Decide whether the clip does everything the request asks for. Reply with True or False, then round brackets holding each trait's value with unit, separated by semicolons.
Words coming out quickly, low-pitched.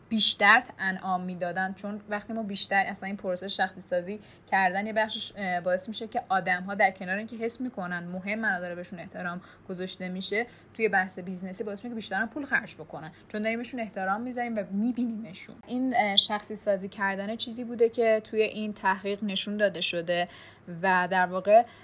False (175 wpm; 200 Hz)